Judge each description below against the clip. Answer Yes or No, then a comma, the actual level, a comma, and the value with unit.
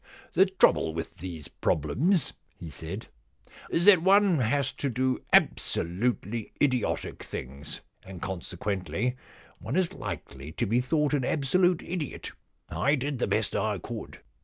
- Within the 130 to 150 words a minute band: Yes, average, 145 wpm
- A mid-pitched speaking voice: No, low, 125 Hz